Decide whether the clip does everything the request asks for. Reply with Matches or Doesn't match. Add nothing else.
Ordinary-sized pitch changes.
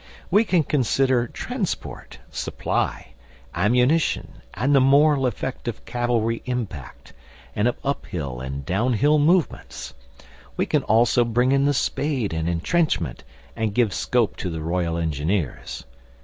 Doesn't match